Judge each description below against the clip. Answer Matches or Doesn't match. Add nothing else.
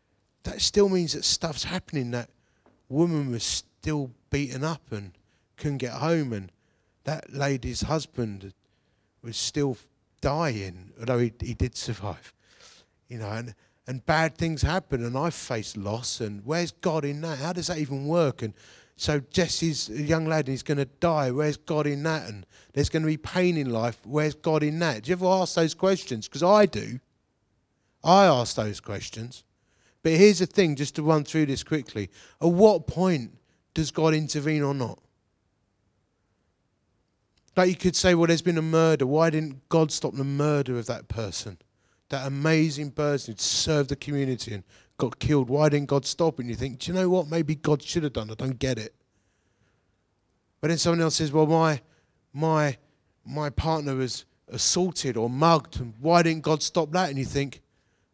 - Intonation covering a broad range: Matches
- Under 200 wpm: Matches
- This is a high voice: Doesn't match